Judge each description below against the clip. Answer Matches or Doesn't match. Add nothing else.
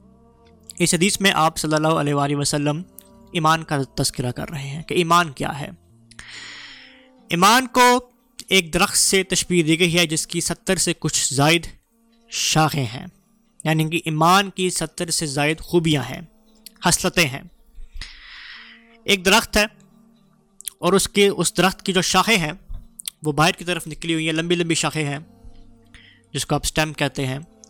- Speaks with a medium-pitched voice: Matches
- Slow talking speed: Doesn't match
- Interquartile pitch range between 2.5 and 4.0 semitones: Doesn't match